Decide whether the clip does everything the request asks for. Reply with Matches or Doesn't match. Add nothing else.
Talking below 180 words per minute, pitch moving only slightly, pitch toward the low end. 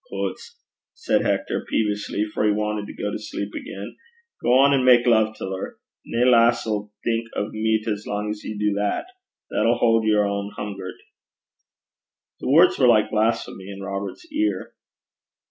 Matches